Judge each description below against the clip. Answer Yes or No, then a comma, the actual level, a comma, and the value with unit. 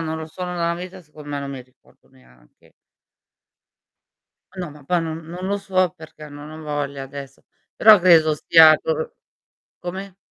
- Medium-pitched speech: Yes, medium, 160 Hz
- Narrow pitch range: No, average, 3.5 semitones